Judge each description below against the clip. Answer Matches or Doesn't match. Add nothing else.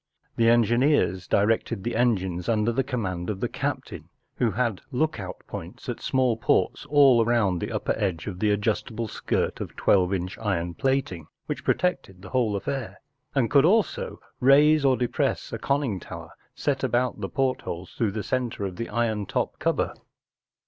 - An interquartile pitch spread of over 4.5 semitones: Matches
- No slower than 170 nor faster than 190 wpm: Matches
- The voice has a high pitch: Doesn't match